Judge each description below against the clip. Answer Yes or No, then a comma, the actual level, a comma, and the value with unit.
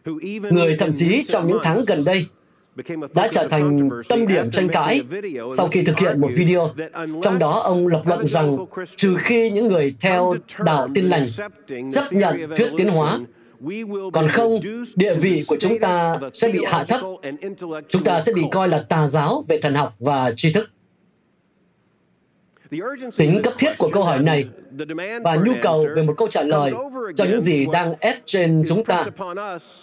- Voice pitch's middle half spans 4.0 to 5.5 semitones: Yes, average, 4.9 semitones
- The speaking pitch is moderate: Yes, medium, 175 Hz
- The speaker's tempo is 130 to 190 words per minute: Yes, average, 175 wpm